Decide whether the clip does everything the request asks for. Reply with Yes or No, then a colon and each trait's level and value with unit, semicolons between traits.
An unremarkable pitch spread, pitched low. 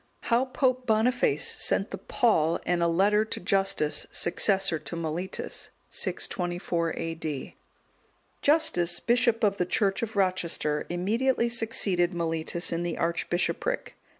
No: average, 4.9 semitones; medium, 185 Hz